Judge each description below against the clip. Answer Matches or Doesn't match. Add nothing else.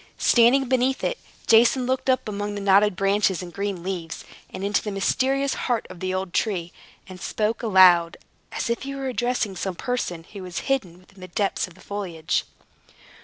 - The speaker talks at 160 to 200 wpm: Matches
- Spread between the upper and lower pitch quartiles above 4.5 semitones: Matches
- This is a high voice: Matches